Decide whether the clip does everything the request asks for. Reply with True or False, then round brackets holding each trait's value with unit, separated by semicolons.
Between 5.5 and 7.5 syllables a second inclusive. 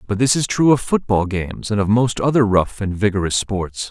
False (5.3 syllables/s)